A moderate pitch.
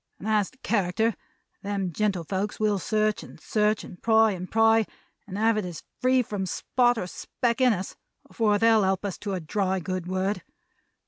No: high, 210 Hz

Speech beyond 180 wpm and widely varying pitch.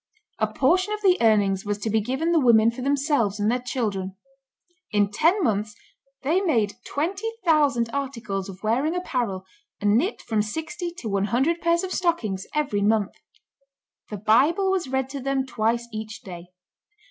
No: average, 170 wpm; wide, 6.8 semitones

